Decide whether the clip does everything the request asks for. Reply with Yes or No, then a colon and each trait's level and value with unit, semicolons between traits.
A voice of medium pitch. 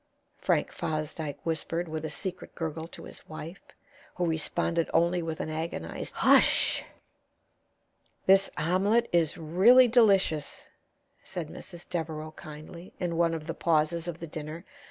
Yes: medium, 165 Hz